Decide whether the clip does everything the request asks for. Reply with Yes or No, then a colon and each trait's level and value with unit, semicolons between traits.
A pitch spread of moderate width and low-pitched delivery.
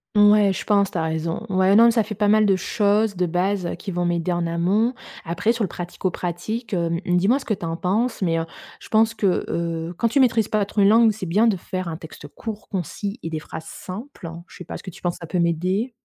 No: average, 3.8 semitones; high, 190 Hz